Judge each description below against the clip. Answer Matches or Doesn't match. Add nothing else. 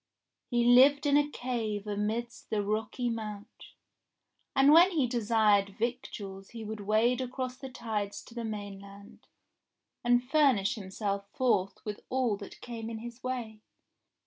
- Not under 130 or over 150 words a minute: Matches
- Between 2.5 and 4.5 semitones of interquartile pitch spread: Matches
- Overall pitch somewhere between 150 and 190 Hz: Doesn't match